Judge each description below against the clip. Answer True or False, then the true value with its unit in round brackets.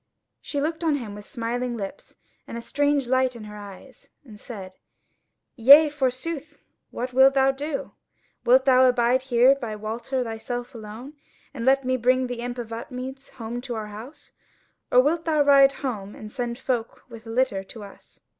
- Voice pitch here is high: True (250 Hz)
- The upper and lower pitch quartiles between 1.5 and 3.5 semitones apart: True (3.0 semitones)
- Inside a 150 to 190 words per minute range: True (180 wpm)